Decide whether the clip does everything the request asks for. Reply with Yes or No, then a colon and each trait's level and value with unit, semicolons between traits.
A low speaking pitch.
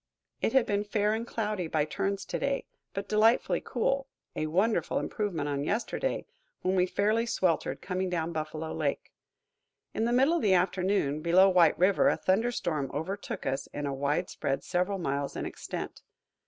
No: high, 190 Hz